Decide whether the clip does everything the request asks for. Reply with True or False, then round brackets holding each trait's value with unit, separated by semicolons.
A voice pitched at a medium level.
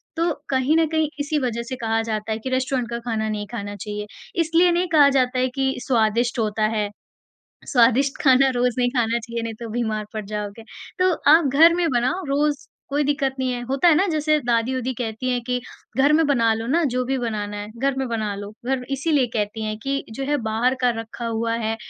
False (250 Hz)